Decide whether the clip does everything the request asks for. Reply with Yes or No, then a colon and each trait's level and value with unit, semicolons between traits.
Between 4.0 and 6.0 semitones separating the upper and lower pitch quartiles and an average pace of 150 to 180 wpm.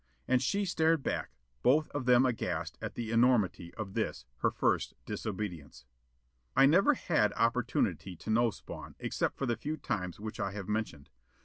Yes: average, 5.0 semitones; average, 170 wpm